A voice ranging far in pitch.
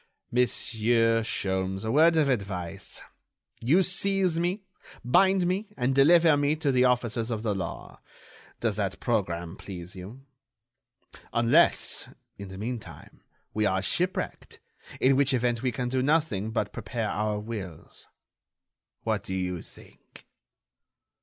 Yes: wide, 6.2 semitones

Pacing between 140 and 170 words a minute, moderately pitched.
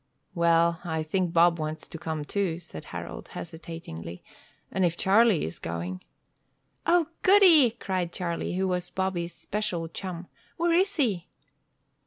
Yes: average, 145 wpm; medium, 175 Hz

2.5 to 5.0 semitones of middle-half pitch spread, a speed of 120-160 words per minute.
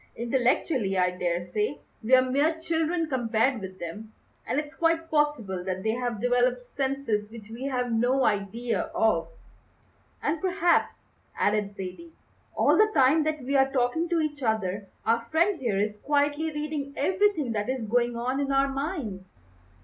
No: wide, 5.5 semitones; average, 155 wpm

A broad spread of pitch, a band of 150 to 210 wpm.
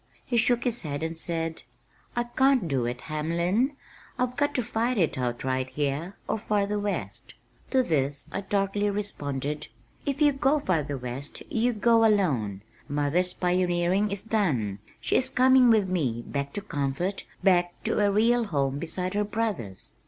Yes: wide, 7.6 semitones; average, 165 wpm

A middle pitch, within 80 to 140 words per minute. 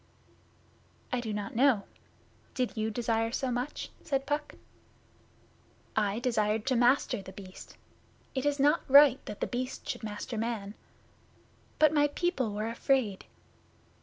No: high, 240 Hz; slow, 135 wpm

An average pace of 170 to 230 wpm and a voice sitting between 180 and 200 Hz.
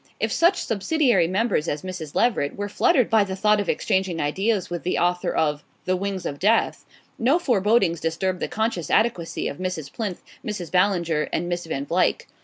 Yes: average, 185 wpm; medium, 185 Hz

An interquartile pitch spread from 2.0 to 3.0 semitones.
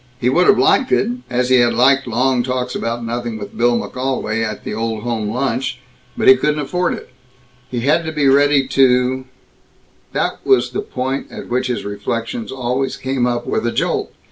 Yes: narrow, 2.4 semitones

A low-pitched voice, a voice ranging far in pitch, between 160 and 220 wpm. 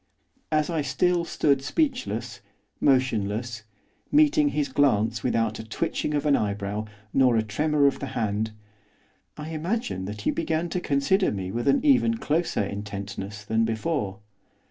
No: low, 130 Hz; wide, 6.9 semitones; average, 145 wpm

